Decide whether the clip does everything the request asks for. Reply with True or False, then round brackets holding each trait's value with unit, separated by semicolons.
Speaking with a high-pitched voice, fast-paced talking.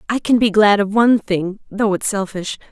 True (205 Hz; 220 wpm)